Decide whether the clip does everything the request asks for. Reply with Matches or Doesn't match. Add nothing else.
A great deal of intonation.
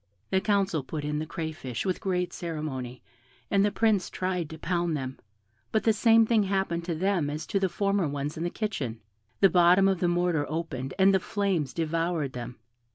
Doesn't match